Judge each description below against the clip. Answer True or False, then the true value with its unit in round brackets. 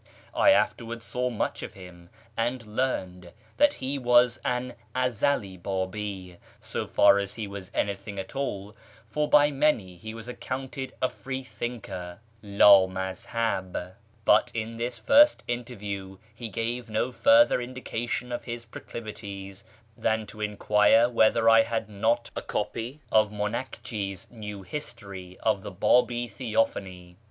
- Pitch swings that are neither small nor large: True (3.6 semitones)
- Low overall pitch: True (110 Hz)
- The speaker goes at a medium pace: True (145 wpm)